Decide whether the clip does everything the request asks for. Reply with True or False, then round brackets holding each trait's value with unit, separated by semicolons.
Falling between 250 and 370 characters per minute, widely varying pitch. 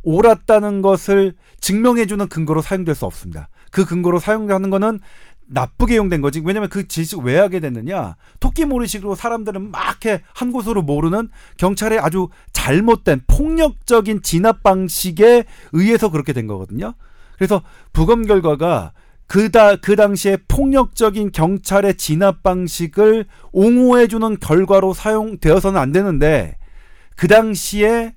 False (315 characters per minute; 4.5 semitones)